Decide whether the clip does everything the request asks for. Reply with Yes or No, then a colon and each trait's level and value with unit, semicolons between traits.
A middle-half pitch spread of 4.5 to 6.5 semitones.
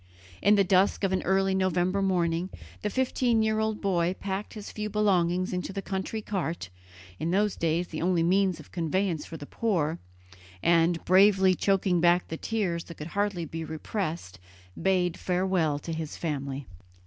No: average, 2.9 semitones